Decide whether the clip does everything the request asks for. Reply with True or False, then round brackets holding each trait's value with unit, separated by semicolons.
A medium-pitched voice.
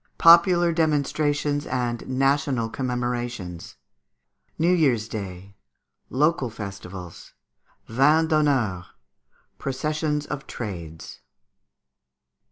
False (130 Hz)